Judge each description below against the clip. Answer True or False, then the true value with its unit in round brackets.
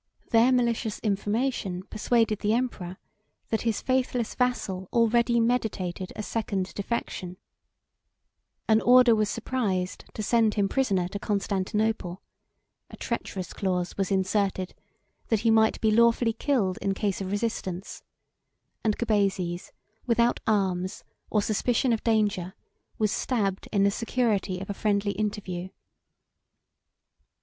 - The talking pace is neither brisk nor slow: False (125 wpm)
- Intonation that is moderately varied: True (3.2 semitones)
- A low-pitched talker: False (210 Hz)